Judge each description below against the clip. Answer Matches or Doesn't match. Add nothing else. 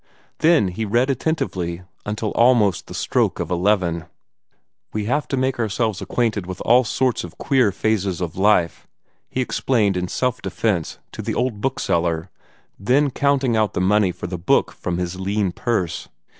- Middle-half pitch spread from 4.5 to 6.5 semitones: Matches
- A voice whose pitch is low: Matches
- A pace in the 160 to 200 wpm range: Matches